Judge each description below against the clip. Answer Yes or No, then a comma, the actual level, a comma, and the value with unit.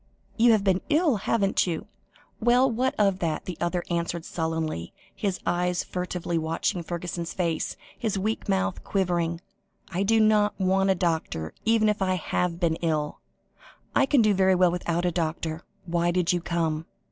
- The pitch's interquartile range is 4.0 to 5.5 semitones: No, average, 2.9 semitones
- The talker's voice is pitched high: No, medium, 180 Hz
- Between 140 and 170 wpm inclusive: Yes, average, 165 wpm